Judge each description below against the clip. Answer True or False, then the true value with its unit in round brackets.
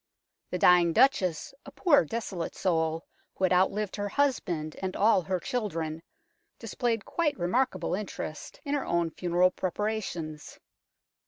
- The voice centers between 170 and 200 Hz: True (185 Hz)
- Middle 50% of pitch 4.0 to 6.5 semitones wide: True (4.6 semitones)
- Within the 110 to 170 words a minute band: True (135 wpm)